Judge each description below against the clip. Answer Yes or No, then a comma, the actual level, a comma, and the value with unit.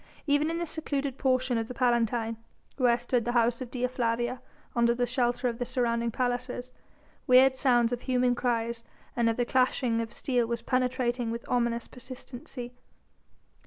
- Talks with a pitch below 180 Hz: No, high, 245 Hz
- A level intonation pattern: Yes, narrow, 1.3 semitones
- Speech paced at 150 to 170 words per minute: Yes, average, 165 wpm